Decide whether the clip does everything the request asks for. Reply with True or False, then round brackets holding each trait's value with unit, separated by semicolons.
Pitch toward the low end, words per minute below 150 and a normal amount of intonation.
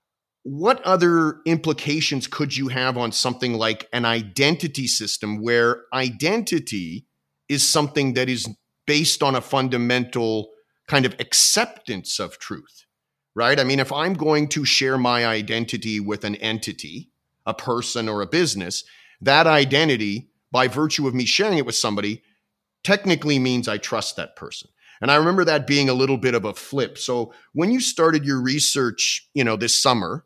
False (130 Hz; 165 wpm; 4.4 semitones)